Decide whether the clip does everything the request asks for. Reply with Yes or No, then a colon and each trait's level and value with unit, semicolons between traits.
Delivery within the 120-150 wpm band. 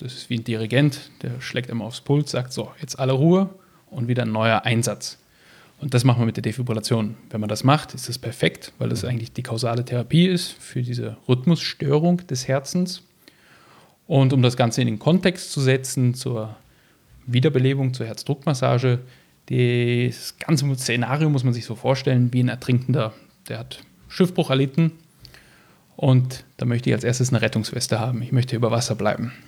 No: average, 180 wpm